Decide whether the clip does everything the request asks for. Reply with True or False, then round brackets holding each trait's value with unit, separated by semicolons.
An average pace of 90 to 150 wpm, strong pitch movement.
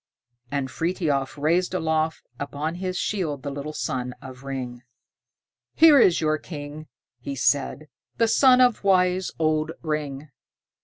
False (135 wpm; 4.3 semitones)